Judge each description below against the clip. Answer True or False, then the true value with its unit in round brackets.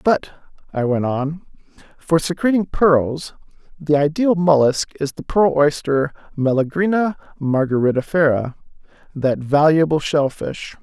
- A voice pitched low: False (150 Hz)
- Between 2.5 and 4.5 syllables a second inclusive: True (4.2 syllables/s)